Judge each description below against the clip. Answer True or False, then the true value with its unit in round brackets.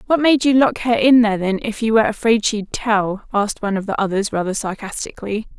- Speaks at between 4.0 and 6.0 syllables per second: False (6.2 syllables/s)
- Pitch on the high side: True (215 Hz)